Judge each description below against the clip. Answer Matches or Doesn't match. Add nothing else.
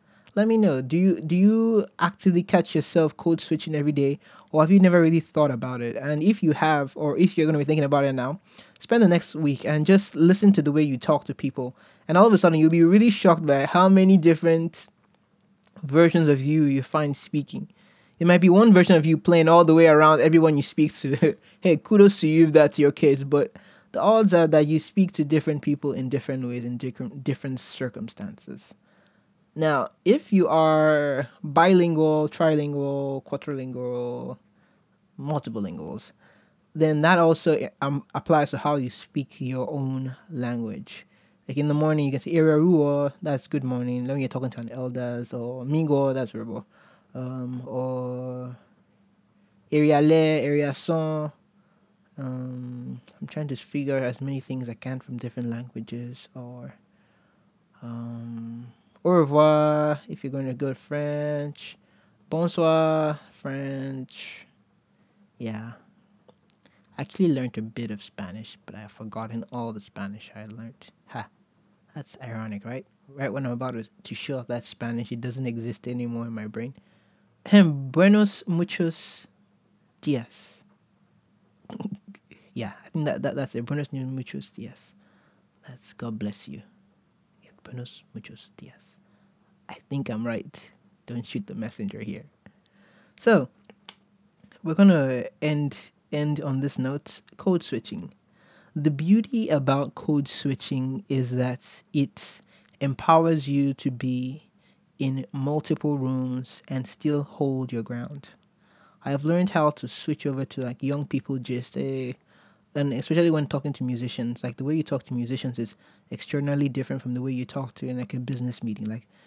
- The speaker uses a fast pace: Doesn't match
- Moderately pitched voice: Matches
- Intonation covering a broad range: Doesn't match